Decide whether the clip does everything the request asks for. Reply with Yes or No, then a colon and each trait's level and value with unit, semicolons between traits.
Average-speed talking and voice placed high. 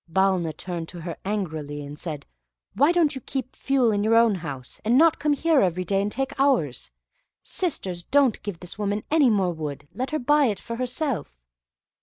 Yes: average, 195 wpm; high, 205 Hz